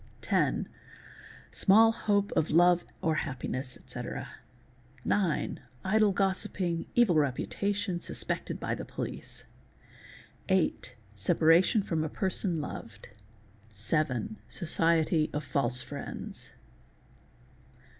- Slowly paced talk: Yes, slow, 80 wpm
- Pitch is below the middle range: No, medium, 165 Hz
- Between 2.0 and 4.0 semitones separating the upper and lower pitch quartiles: No, wide, 5.5 semitones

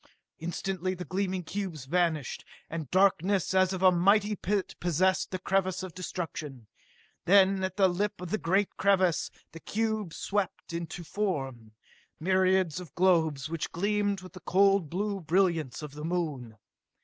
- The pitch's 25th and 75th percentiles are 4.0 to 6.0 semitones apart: No, average, 2.9 semitones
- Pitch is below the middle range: No, medium, 185 Hz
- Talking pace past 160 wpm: No, average, 150 wpm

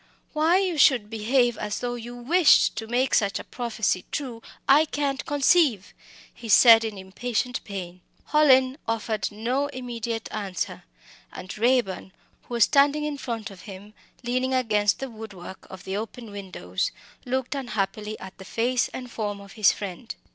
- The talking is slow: No, average, 160 wpm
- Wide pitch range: No, average, 4.0 semitones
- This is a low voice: No, high, 230 Hz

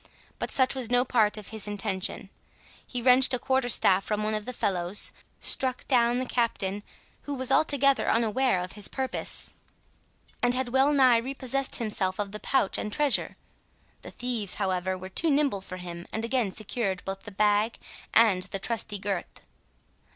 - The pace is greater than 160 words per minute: Yes, average, 175 wpm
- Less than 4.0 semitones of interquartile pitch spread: No, average, 4.6 semitones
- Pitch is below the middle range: No, high, 225 Hz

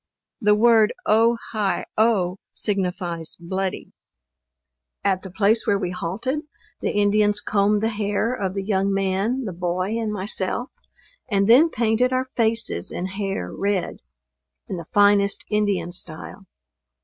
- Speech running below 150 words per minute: Yes, slow, 135 wpm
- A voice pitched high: Yes, high, 205 Hz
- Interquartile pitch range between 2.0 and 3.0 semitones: Yes, average, 2.7 semitones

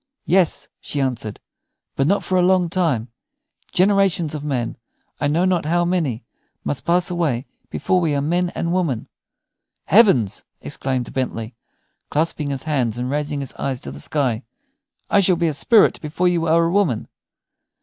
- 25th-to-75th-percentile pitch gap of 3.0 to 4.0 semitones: No, average, 5.2 semitones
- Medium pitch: Yes, medium, 155 Hz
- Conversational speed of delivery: Yes, average, 165 wpm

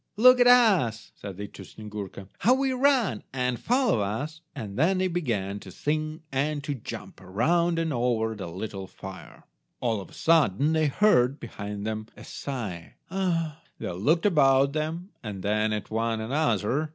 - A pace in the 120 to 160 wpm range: No, average, 170 wpm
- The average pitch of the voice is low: Yes, low, 130 Hz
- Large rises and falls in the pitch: Yes, wide, 7.7 semitones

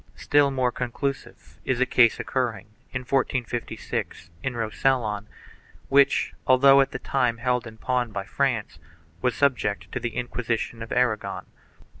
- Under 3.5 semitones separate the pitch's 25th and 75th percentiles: Yes, narrow, 2.6 semitones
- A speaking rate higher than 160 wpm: No, average, 140 wpm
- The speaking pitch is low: Yes, low, 125 Hz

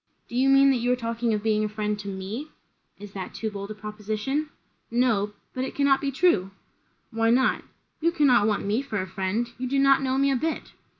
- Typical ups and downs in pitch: Yes, average, 4.5 semitones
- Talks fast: Yes, fast, 225 wpm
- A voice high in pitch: Yes, high, 230 Hz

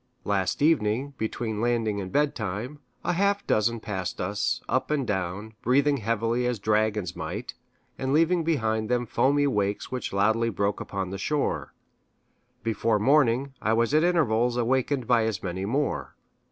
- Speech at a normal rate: Yes, average, 155 wpm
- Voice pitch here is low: Yes, low, 115 Hz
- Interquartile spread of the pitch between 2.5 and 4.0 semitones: No, average, 4.7 semitones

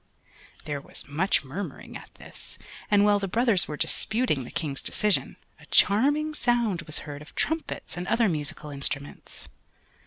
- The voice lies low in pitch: No, medium, 185 Hz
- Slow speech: No, average, 155 wpm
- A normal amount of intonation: No, wide, 7.4 semitones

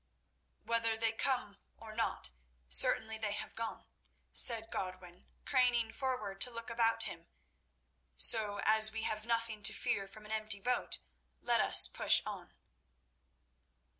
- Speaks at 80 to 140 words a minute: Yes, slow, 135 wpm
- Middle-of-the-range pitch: No, high, 220 Hz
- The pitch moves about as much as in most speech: No, narrow, 1.7 semitones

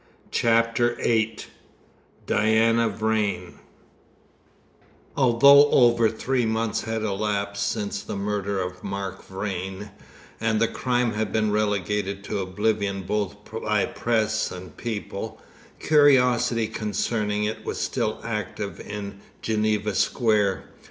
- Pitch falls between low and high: No, low, 105 Hz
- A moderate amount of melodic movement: No, narrow, 2.1 semitones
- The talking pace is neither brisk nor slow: No, slow, 110 wpm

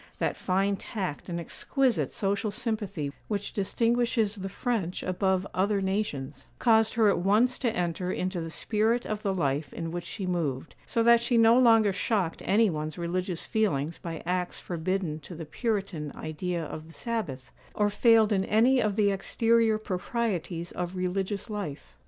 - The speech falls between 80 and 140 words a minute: No, average, 165 wpm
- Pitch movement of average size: Yes, average, 4.3 semitones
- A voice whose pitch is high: Yes, high, 195 Hz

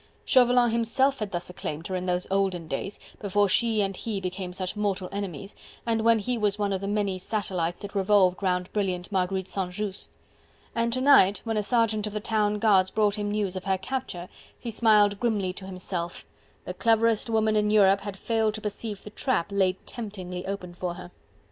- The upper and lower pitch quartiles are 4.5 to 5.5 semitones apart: No, narrow, 2.6 semitones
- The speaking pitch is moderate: No, high, 200 Hz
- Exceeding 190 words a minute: Yes, average, 200 wpm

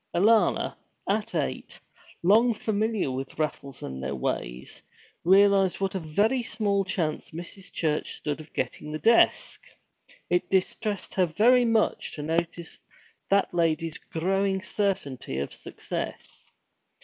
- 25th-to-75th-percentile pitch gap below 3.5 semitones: No, average, 4.7 semitones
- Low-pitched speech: No, medium, 185 Hz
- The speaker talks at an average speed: No, slow, 125 wpm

